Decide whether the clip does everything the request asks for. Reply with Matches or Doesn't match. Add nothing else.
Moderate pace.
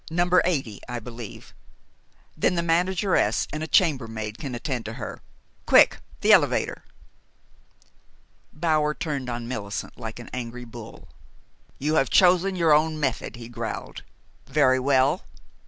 Doesn't match